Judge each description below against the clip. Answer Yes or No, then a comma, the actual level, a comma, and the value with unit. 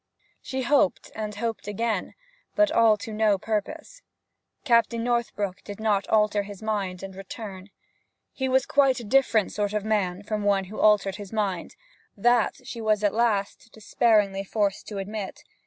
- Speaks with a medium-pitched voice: No, high, 210 Hz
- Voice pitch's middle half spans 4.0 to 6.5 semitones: No, narrow, 2.5 semitones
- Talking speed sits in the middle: Yes, average, 160 wpm